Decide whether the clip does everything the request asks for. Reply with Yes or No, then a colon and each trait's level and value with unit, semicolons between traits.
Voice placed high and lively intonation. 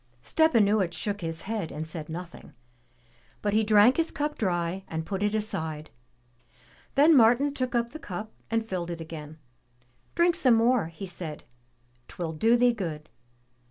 Yes: high, 205 Hz; wide, 6.1 semitones